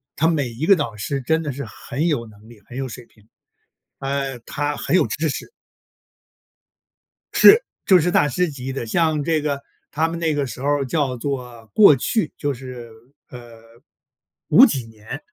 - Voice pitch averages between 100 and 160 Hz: Yes, medium, 140 Hz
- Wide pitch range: No, average, 4.4 semitones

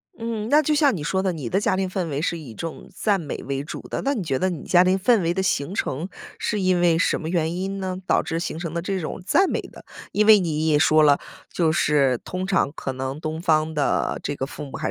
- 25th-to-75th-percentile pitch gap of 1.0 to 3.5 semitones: No, average, 4.1 semitones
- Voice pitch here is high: No, medium, 170 Hz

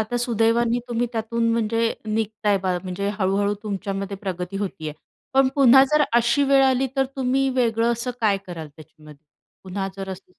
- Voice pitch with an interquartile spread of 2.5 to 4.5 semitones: Yes, average, 3.5 semitones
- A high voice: Yes, high, 220 Hz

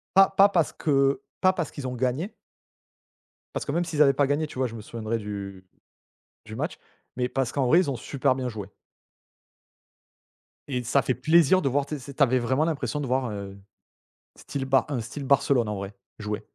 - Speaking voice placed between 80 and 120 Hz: No, low, 135 Hz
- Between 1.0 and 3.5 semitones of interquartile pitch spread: No, average, 3.9 semitones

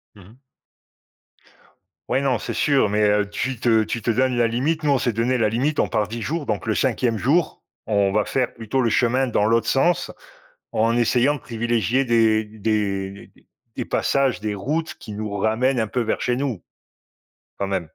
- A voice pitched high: No, low, 115 Hz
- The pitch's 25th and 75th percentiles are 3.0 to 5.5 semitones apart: Yes, average, 3.4 semitones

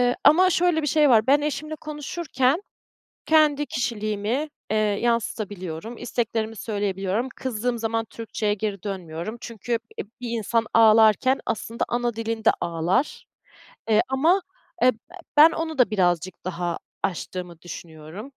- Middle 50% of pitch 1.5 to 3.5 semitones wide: No, average, 4.7 semitones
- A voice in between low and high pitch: No, high, 225 Hz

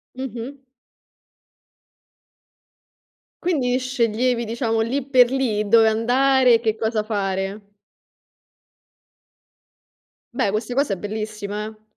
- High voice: Yes, high, 225 Hz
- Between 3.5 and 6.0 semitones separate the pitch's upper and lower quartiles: No, average, 3.0 semitones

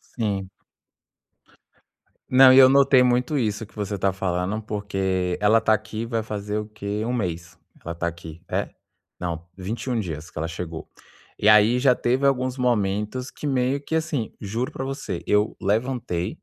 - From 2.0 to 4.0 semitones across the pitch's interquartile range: No, average, 4.8 semitones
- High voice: No, low, 105 Hz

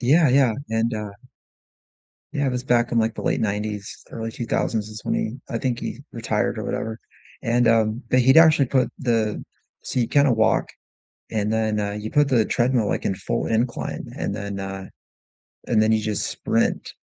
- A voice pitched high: No, low, 115 Hz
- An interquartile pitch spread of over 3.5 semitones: No, narrow, 2.6 semitones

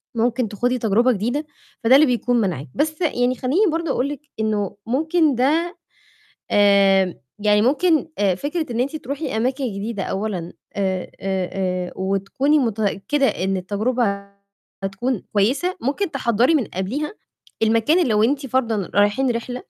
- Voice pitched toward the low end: No, high, 235 Hz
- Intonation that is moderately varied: No, wide, 5.8 semitones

